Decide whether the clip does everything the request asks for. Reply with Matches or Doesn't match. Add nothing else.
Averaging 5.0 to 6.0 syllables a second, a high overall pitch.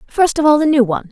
Doesn't match